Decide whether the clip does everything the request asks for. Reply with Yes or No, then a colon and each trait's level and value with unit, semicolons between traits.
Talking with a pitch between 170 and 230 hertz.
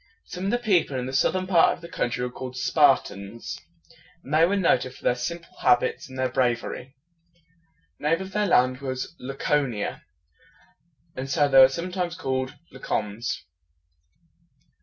No: low, 135 Hz